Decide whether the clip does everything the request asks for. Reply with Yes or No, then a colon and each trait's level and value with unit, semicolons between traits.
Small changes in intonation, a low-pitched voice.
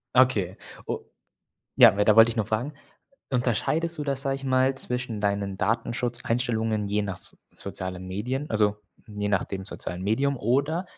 No: average, 4.2 semitones; low, 115 Hz